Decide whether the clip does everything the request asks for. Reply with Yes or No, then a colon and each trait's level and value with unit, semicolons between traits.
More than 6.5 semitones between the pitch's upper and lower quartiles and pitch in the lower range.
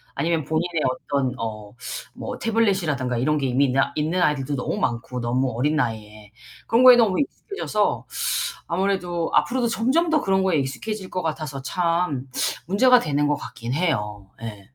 No: wide, 7.0 semitones; medium, 150 Hz